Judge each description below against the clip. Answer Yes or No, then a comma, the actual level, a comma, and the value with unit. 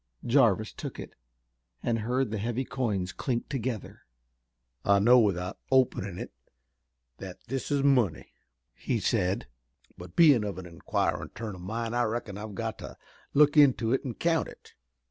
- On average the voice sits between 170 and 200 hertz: No, low, 115 Hz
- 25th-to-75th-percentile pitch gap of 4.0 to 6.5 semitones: Yes, average, 4.6 semitones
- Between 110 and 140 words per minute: No, average, 160 wpm